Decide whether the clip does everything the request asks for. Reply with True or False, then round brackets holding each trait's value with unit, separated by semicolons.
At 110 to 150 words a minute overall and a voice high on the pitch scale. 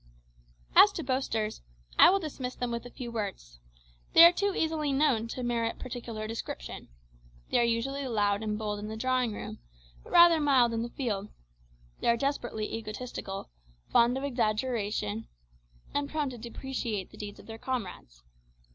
False (165 wpm; 235 Hz)